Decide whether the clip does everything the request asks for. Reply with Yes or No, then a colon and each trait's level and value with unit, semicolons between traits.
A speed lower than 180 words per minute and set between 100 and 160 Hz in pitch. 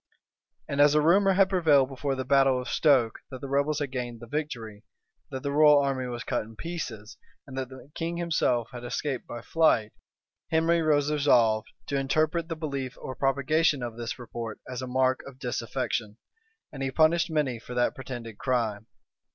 No: average, 185 wpm; low, 135 Hz